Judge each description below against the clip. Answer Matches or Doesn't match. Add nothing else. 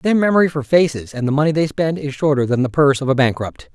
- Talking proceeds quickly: Matches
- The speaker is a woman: Doesn't match